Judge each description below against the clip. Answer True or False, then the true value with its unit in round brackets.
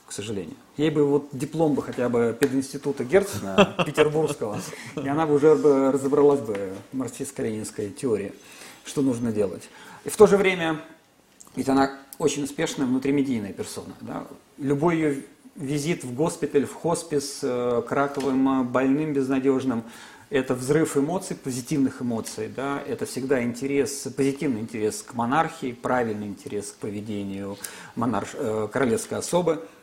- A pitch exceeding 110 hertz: True (140 Hz)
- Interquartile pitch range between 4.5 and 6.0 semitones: False (3.3 semitones)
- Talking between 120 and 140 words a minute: True (135 wpm)